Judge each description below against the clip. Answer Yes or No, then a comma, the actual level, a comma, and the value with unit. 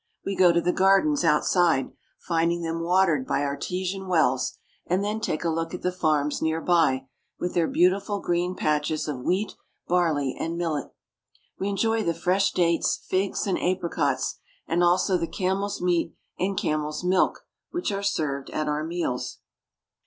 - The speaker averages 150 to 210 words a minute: Yes, average, 160 wpm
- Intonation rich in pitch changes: No, average, 3.3 semitones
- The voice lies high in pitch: No, medium, 175 Hz